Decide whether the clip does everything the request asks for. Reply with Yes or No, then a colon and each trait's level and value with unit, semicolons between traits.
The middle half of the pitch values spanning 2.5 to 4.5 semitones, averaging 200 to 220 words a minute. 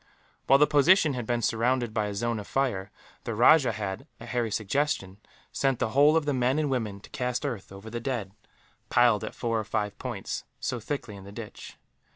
Yes: average, 4.1 semitones; fast, 205 wpm